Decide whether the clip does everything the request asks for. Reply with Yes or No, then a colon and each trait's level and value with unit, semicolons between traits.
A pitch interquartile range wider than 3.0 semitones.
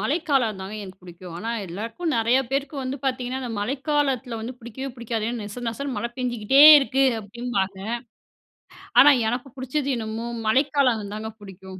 Yes: average, 3.9 semitones